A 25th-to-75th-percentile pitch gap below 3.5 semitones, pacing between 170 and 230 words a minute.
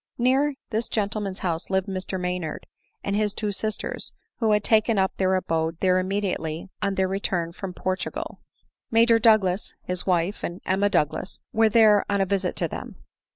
Yes: average, 2.7 semitones; average, 175 wpm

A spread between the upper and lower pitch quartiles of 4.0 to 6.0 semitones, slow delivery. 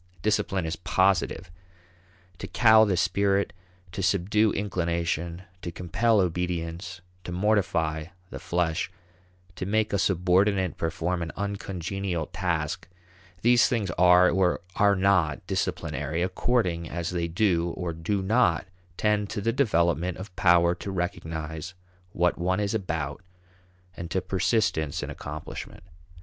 No: average, 2.9 semitones; slow, 130 wpm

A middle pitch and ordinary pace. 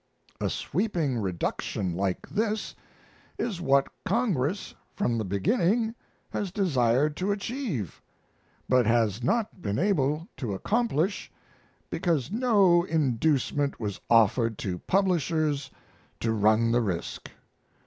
No: medium, 145 Hz; slow, 110 wpm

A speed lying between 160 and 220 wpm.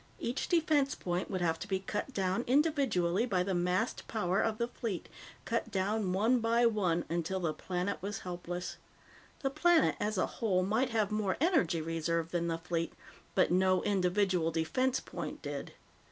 Yes: average, 170 wpm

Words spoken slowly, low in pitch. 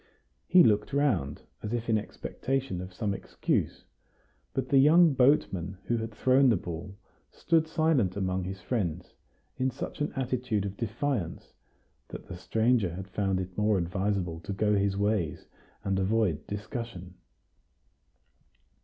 No: average, 145 wpm; low, 105 Hz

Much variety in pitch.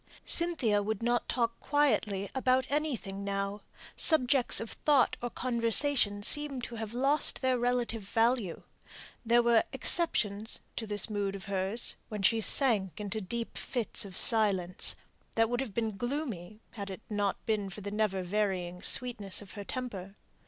No: average, 3.6 semitones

